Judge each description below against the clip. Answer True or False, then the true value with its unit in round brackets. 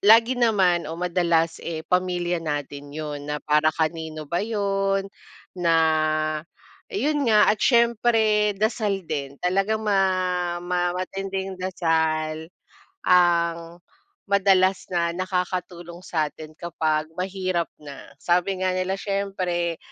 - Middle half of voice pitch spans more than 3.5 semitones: False (3.0 semitones)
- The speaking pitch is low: False (180 Hz)